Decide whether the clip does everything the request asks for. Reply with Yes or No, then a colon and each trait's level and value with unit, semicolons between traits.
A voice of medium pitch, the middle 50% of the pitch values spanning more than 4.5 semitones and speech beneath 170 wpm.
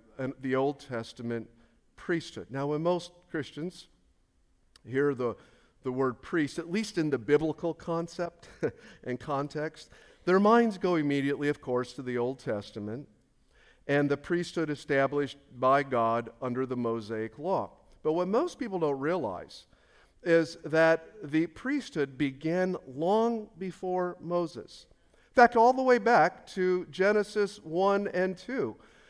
Yes: medium, 155 Hz; wide, 5.6 semitones; average, 140 wpm